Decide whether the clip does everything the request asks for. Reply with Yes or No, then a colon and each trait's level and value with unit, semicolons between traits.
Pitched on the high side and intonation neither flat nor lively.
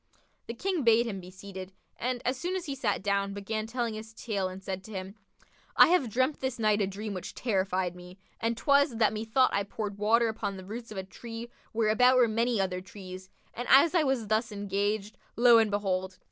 Yes: high, 215 Hz; average, 3.4 semitones